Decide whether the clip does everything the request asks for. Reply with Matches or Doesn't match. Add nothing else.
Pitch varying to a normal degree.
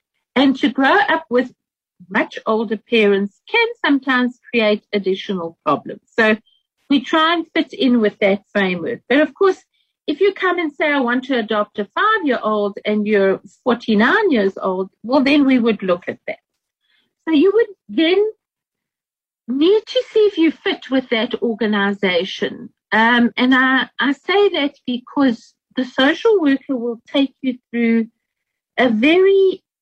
Doesn't match